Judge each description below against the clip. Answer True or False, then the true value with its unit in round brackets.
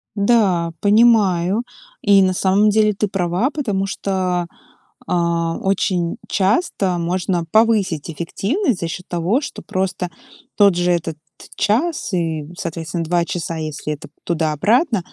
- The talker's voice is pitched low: False (185 Hz)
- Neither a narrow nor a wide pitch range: True (3.6 semitones)